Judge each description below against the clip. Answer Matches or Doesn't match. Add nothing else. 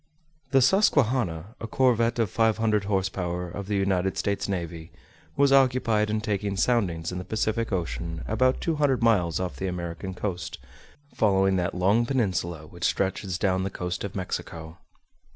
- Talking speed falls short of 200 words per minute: Matches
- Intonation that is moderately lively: Matches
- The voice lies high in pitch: Doesn't match